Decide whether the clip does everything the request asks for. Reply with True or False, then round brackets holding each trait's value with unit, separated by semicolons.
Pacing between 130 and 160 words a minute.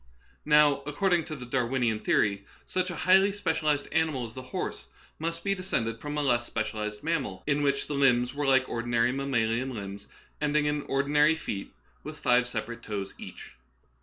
False (170 wpm)